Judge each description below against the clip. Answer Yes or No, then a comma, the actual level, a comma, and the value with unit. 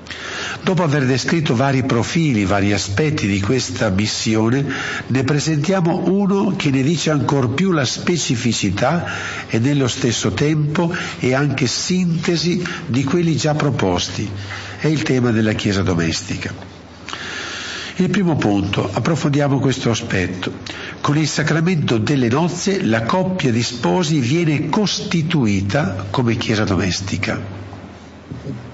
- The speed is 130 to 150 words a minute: No, average, 120 wpm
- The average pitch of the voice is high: No, low, 135 Hz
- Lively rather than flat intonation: Yes, wide, 6.8 semitones